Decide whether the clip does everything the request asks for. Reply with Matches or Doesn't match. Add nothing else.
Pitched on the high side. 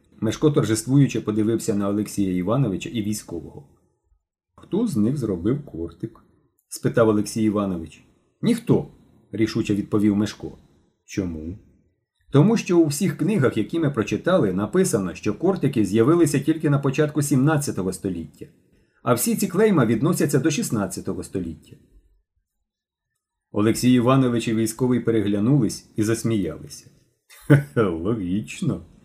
Doesn't match